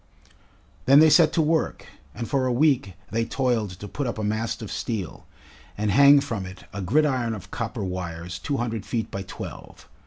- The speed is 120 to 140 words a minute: No, average, 190 wpm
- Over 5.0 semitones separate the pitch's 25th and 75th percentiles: Yes, wide, 5.6 semitones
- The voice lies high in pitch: No, low, 115 Hz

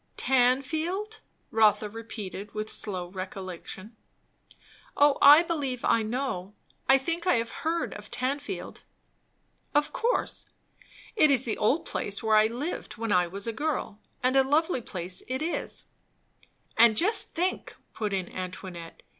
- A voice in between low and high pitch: No, high, 235 Hz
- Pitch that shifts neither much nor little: No, wide, 6.2 semitones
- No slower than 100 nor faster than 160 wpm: Yes, average, 145 wpm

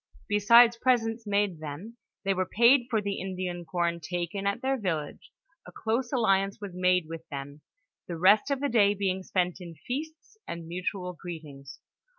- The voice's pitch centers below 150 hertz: No, high, 195 Hz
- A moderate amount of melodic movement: Yes, average, 4.6 semitones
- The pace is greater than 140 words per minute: Yes, average, 165 wpm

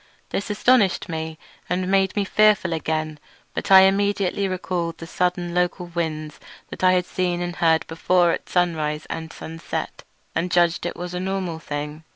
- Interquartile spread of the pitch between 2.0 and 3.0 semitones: Yes, narrow, 2.4 semitones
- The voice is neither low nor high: Yes, medium, 175 Hz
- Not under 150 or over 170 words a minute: Yes, average, 165 wpm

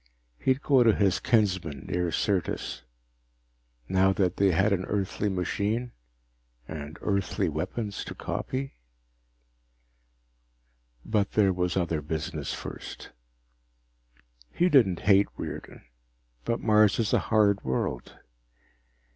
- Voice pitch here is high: No, low, 100 Hz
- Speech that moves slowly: Yes, slow, 110 wpm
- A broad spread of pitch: No, average, 3.2 semitones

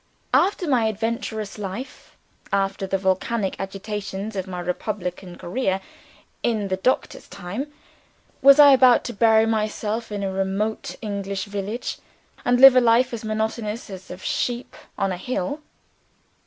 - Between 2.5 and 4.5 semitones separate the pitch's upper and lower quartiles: Yes, average, 3.4 semitones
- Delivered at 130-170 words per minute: Yes, average, 155 wpm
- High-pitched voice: Yes, high, 210 Hz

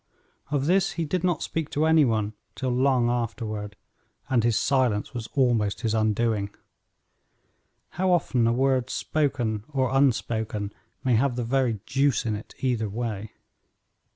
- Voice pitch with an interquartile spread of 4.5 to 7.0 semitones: No, average, 3.8 semitones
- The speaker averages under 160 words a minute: Yes, average, 150 wpm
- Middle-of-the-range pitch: No, low, 120 Hz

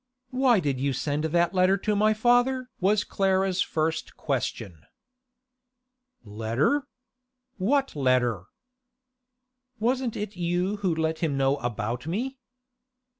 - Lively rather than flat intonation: Yes, wide, 7.5 semitones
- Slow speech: Yes, slow, 115 wpm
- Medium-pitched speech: Yes, medium, 180 Hz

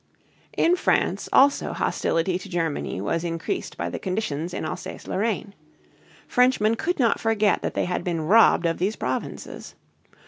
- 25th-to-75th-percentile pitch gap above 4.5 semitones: Yes, average, 5.2 semitones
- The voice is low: No, high, 190 Hz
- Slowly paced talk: No, average, 150 wpm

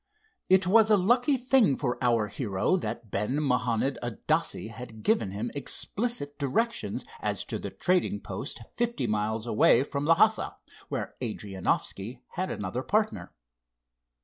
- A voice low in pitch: Yes, low, 130 Hz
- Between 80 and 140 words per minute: Yes, slow, 135 wpm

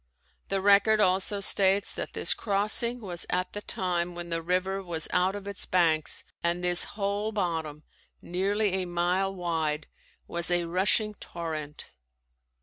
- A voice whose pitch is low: No, medium, 185 Hz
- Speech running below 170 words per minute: Yes, average, 145 wpm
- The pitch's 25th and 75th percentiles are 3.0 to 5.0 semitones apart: No, narrow, 2.6 semitones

